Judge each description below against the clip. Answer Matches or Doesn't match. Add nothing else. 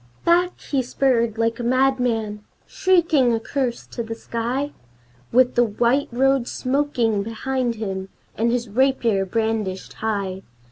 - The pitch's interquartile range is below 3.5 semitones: Matches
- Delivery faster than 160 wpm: Doesn't match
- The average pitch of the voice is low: Doesn't match